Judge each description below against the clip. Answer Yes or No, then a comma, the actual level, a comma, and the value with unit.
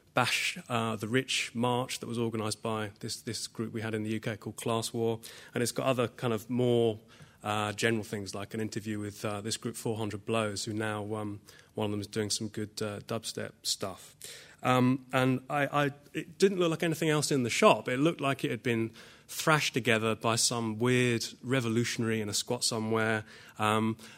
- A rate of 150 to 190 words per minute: No, fast, 205 wpm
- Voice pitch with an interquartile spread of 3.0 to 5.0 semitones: No, narrow, 2.5 semitones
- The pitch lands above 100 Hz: Yes, low, 115 Hz